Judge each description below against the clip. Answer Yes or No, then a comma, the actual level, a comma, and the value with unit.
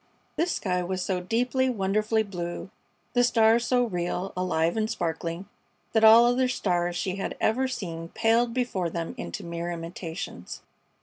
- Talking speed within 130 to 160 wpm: Yes, average, 150 wpm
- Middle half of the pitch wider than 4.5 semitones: Yes, average, 5.0 semitones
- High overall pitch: Yes, high, 195 Hz